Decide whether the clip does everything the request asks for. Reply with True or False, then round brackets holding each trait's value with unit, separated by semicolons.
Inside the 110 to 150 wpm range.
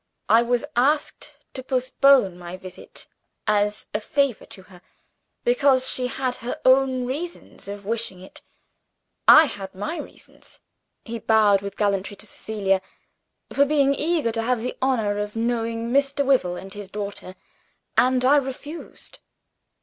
True (145 wpm)